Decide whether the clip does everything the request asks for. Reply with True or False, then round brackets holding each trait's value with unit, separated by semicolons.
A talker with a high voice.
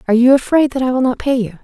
True (250 Hz)